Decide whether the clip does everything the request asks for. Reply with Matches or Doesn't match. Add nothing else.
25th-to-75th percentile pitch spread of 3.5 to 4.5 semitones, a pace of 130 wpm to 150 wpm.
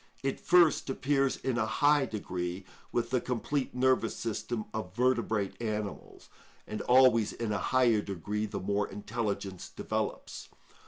Matches